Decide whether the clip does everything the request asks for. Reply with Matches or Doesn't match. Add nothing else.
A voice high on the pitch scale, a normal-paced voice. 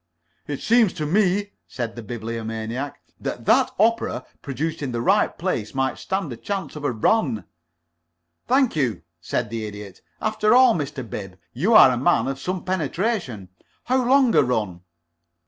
Doesn't match